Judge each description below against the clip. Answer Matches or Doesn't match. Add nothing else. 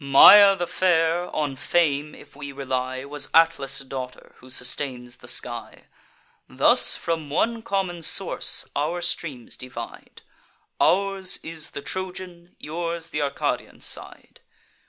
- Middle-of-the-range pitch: Matches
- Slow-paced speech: Matches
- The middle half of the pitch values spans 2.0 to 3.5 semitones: Doesn't match